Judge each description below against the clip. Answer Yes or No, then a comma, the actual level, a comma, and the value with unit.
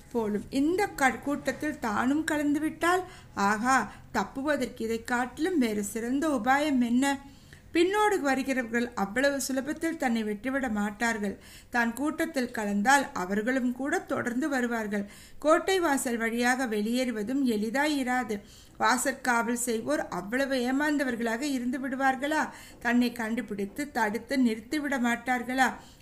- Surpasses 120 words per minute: No, average, 105 wpm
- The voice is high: Yes, very high, 260 Hz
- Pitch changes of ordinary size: Yes, average, 3.5 semitones